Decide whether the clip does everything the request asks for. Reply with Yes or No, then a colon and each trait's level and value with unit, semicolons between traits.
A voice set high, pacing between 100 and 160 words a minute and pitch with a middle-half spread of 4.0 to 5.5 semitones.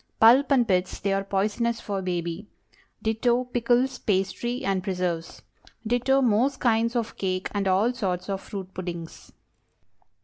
Yes: high, 205 Hz; average, 140 wpm; average, 4.3 semitones